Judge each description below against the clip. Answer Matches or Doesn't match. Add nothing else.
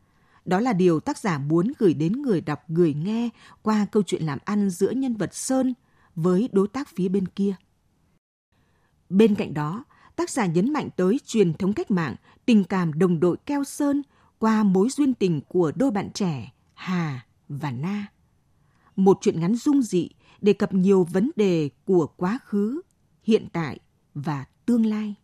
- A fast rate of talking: Doesn't match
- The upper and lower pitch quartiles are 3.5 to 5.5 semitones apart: Matches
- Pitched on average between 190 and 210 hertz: Matches